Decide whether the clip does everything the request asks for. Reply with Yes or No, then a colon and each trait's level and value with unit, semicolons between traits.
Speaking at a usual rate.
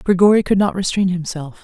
Yes: average, 185 wpm